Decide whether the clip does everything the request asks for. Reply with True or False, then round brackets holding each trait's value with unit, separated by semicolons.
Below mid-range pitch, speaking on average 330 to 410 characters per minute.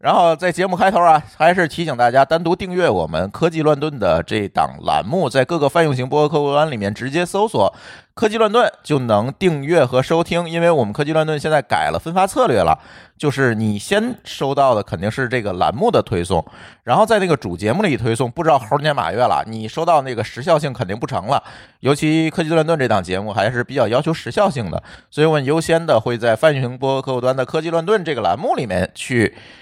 False (150 Hz; 350 characters per minute)